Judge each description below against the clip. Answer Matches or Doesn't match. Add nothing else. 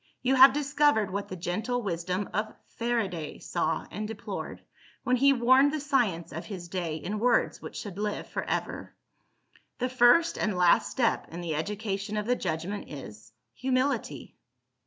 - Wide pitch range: Matches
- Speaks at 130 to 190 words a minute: Matches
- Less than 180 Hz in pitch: Doesn't match